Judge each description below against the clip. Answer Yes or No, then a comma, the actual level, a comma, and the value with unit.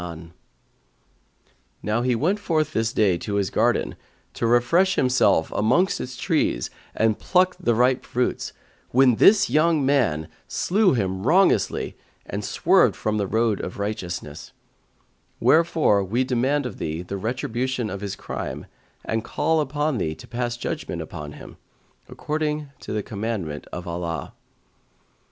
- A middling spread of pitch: No, wide, 6.7 semitones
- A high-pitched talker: No, low, 120 Hz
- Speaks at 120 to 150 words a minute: Yes, average, 140 wpm